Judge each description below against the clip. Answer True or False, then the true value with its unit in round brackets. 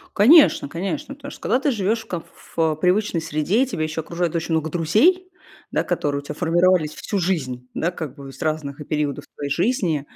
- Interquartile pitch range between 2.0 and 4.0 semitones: False (5.2 semitones)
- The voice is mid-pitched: True (170 Hz)